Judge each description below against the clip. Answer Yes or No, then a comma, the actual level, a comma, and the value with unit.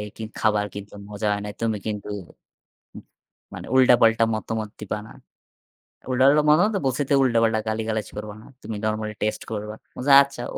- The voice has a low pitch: Yes, low, 110 Hz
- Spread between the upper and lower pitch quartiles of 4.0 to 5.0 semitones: No, average, 2.8 semitones